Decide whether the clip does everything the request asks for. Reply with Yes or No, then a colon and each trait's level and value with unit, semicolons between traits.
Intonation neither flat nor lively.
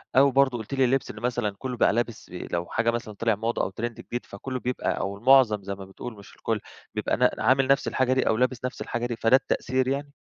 Yes: average, 3.2 semitones